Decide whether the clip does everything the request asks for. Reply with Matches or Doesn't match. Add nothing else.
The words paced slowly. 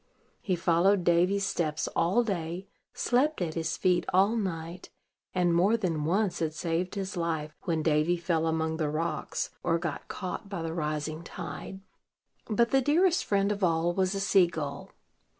Doesn't match